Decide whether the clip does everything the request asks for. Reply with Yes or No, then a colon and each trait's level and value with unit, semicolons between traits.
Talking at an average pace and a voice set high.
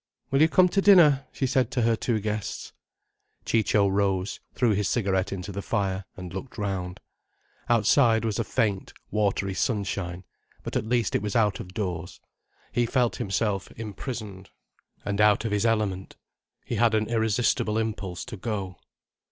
No: average, 160 wpm; low, 105 Hz